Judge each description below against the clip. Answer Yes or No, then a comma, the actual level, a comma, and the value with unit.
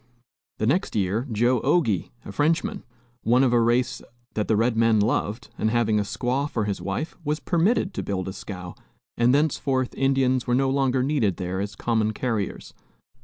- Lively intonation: No, average, 4.2 semitones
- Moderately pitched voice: No, low, 120 Hz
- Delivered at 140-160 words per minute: No, average, 180 wpm